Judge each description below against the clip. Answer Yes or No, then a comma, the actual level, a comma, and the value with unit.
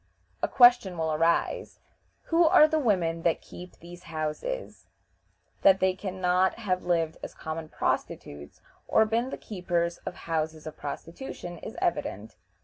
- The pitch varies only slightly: No, average, 4.1 semitones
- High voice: No, medium, 175 Hz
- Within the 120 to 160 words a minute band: Yes, average, 145 wpm